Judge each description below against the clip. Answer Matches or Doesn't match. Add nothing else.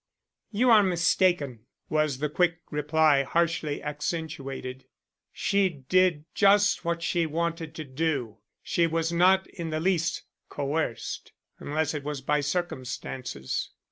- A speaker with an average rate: Doesn't match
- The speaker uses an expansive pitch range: Doesn't match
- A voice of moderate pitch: Matches